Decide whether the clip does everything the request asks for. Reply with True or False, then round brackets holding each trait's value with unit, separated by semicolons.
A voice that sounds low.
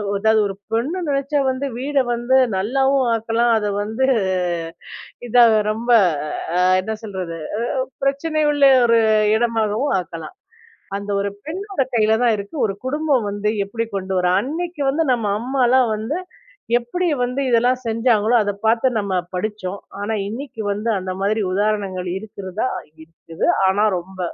False (225 Hz)